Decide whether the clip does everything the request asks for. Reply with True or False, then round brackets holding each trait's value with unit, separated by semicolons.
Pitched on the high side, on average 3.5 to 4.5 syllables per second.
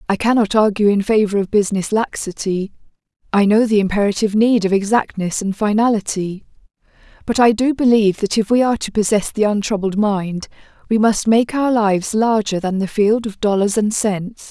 False (210 Hz; 5.4 syllables/s)